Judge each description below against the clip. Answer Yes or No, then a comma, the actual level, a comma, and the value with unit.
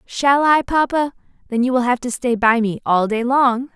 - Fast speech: Yes, fast, 210 wpm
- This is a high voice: Yes, very high, 250 Hz